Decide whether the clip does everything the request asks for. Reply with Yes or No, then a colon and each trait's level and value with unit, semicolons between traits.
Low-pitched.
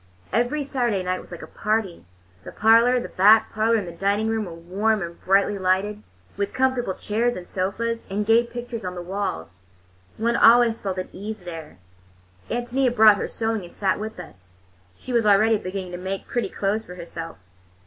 No: high, 205 Hz